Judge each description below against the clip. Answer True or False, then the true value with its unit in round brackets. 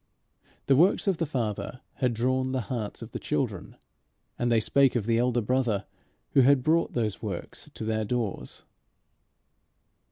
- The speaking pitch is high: False (125 Hz)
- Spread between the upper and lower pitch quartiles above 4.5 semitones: False (2.9 semitones)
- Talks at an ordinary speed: True (160 wpm)